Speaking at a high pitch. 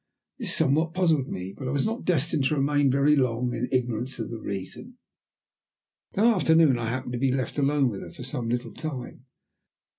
No: low, 135 Hz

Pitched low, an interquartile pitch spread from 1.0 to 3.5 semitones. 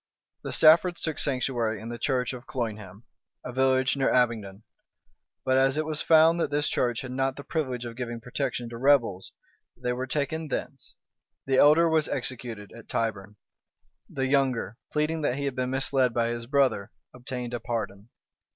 Yes: low, 130 Hz; average, 3.1 semitones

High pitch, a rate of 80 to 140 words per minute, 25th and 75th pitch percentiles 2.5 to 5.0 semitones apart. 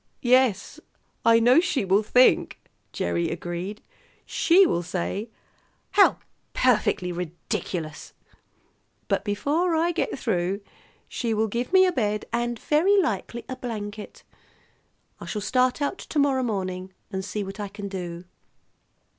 No: high, 220 Hz; slow, 135 wpm; wide, 5.4 semitones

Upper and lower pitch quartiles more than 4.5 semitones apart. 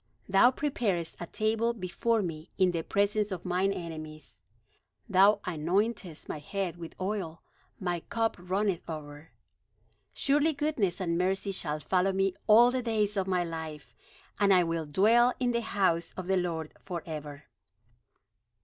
No: average, 4.2 semitones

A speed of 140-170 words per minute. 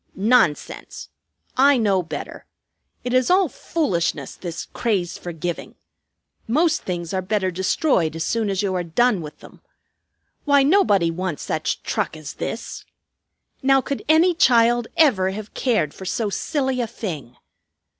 Yes: average, 145 wpm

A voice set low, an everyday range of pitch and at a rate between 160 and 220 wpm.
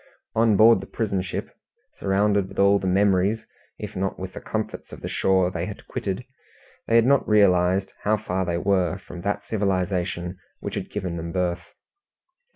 No: very low, 95 Hz; narrow, 2.1 semitones; average, 175 wpm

